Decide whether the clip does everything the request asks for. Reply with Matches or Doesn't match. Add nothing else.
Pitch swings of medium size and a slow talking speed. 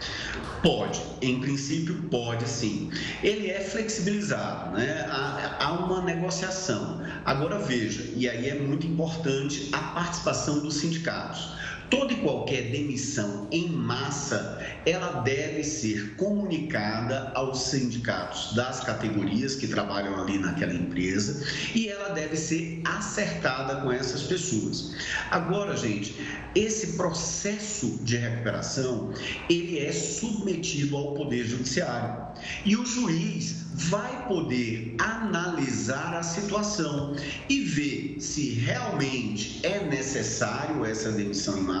Doesn't match